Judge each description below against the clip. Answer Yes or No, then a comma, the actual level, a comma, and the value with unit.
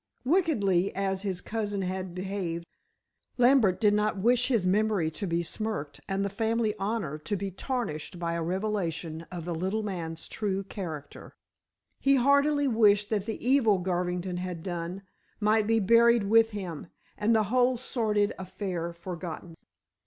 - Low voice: No, high, 195 Hz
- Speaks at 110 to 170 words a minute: Yes, average, 155 wpm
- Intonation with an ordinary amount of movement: Yes, average, 3.9 semitones